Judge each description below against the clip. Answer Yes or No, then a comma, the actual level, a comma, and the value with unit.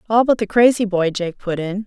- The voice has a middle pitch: No, high, 205 Hz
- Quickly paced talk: Yes, fast, 260 wpm